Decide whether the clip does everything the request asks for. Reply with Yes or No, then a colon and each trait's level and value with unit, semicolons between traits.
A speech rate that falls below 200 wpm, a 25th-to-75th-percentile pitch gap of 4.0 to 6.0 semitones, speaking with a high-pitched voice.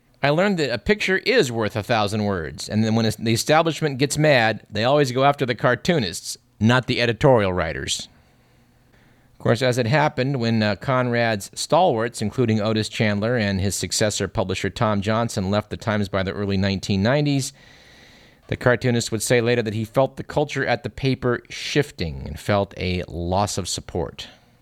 No: average, 175 wpm; average, 4.3 semitones; low, 115 Hz